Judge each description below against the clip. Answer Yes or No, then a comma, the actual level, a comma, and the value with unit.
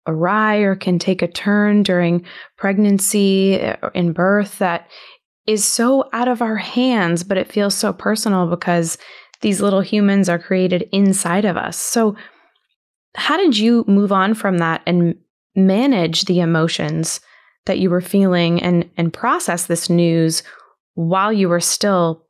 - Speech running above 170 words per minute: No, average, 155 wpm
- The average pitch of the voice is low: No, high, 190 Hz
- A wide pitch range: No, average, 3.2 semitones